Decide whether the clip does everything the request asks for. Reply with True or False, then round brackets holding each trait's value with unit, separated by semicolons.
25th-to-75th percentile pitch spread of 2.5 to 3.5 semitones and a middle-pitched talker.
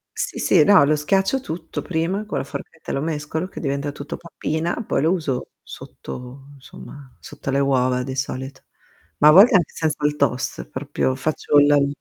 True (2.9 semitones; 145 Hz)